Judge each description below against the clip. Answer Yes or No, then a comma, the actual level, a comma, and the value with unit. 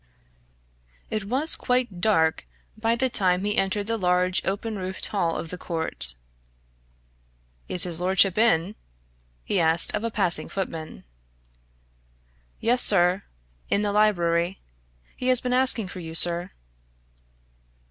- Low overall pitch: No, high, 190 Hz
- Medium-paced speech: No, slow, 130 wpm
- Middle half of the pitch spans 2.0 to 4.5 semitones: Yes, average, 3.9 semitones